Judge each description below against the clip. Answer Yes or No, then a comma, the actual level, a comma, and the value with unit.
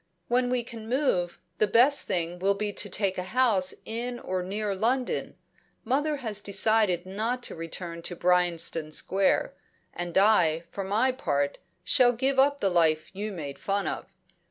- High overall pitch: Yes, high, 200 Hz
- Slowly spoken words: No, average, 165 wpm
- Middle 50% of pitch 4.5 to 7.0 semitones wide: Yes, wide, 5.4 semitones